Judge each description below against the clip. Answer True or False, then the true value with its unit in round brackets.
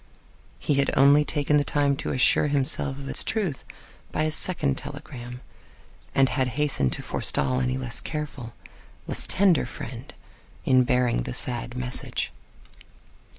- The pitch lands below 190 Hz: True (135 Hz)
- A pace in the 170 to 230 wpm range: False (145 wpm)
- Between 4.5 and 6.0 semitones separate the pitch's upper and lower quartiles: False (2.7 semitones)